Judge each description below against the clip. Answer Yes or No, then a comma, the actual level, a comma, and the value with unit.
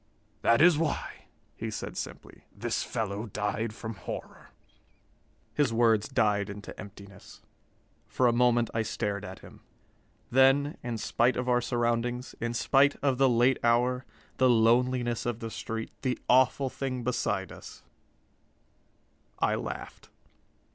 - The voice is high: No, low, 120 Hz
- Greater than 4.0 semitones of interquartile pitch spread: No, narrow, 2.4 semitones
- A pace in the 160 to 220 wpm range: No, slow, 135 wpm